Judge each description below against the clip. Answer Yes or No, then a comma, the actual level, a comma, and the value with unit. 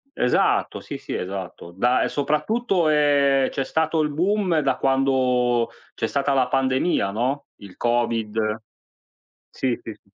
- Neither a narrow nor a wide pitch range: Yes, average, 4.0 semitones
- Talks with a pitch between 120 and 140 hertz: Yes, low, 135 Hz